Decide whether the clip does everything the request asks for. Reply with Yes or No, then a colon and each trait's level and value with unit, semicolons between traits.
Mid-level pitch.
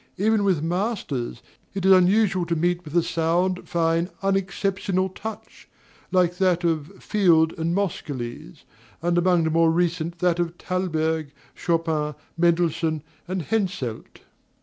Yes: medium, 175 Hz